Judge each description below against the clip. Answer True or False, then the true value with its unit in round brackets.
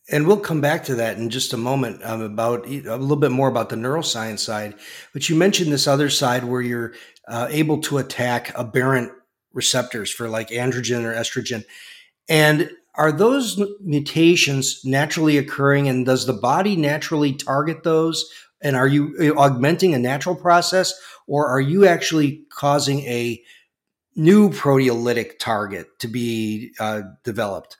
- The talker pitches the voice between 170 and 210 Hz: False (140 Hz)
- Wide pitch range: False (4.3 semitones)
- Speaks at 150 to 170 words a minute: True (155 wpm)